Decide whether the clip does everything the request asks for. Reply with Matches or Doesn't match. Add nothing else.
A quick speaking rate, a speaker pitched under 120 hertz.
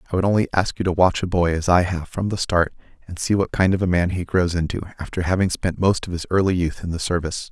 Matches